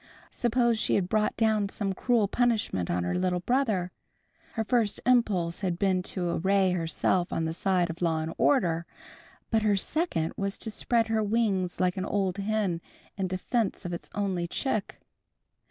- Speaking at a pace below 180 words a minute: Yes, average, 170 wpm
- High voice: Yes, high, 195 Hz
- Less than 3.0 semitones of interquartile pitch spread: No, average, 3.8 semitones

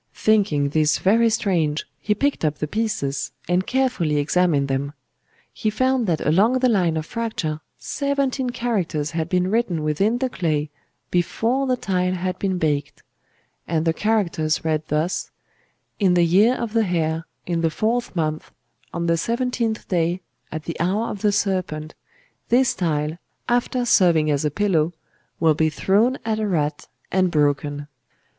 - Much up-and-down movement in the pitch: Yes, wide, 6.0 semitones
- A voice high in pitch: No, medium, 180 Hz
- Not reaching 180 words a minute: Yes, average, 160 wpm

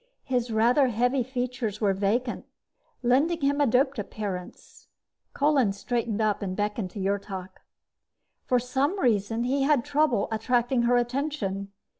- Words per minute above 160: No, slow, 135 wpm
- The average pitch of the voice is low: No, high, 240 Hz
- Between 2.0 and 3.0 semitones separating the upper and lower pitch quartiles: No, average, 4.2 semitones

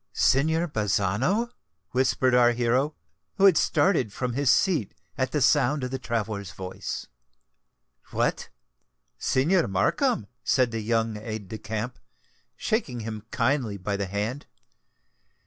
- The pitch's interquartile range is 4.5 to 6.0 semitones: Yes, average, 5.0 semitones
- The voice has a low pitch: Yes, low, 120 Hz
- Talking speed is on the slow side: Yes, slow, 130 wpm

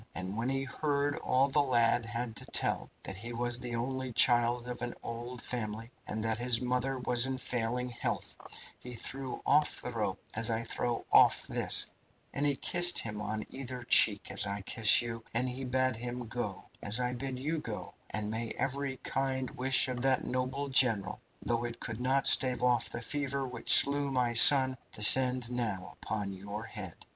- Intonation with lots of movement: No, narrow, 2.4 semitones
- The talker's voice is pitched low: Yes, low, 125 Hz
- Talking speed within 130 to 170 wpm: No, average, 190 wpm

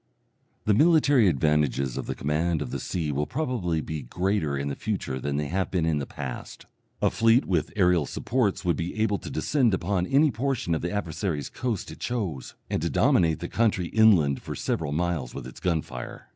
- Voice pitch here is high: No, very low, 85 Hz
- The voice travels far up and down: Yes, wide, 6.3 semitones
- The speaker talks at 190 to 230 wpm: Yes, average, 200 wpm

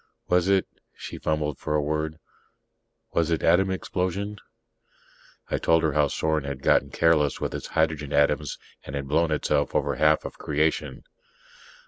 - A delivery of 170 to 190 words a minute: No, average, 160 wpm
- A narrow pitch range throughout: Yes, narrow, 2.0 semitones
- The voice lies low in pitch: Yes, very low, 80 Hz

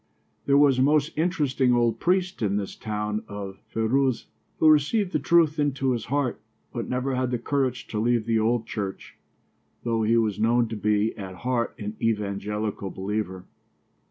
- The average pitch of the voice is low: Yes, low, 115 Hz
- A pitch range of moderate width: Yes, average, 4.5 semitones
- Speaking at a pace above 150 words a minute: Yes, average, 170 wpm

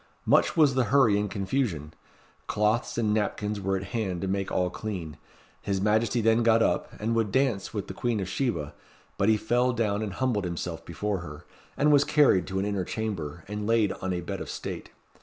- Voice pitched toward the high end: No, low, 105 Hz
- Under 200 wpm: No, fast, 205 wpm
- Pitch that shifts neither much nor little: Yes, average, 3.4 semitones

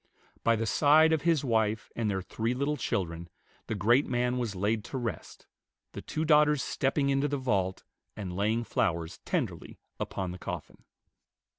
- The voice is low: Yes, low, 115 Hz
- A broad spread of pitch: Yes, wide, 5.7 semitones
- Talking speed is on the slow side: No, average, 165 wpm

